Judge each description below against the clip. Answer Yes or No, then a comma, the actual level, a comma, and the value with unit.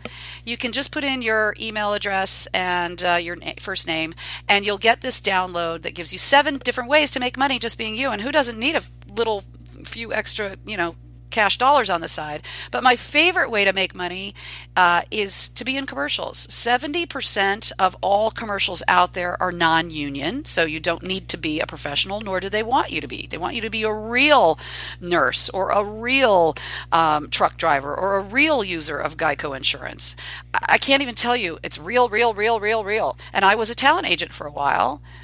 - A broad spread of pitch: Yes, wide, 6.4 semitones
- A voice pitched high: Yes, high, 205 Hz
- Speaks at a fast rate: Yes, fast, 210 wpm